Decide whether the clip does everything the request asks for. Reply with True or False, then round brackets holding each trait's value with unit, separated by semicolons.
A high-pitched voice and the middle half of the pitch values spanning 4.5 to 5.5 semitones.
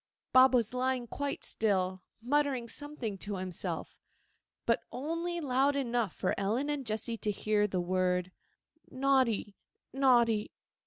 True (235 Hz; 4.8 semitones)